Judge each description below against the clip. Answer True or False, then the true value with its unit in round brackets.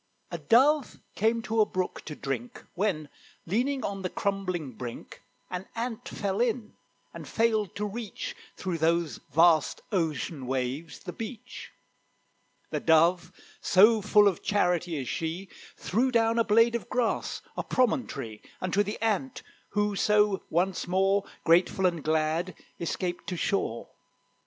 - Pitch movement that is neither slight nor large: True (4.9 semitones)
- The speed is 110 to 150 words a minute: True (140 wpm)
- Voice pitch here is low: False (190 Hz)